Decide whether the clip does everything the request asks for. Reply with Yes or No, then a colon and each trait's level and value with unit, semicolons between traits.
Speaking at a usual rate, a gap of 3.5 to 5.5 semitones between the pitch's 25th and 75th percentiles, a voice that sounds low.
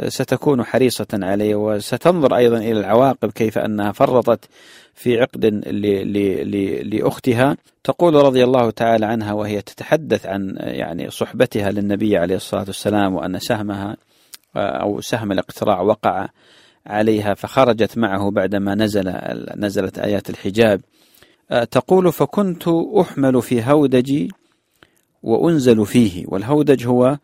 No: slow, 115 wpm; average, 4.3 semitones; low, 110 Hz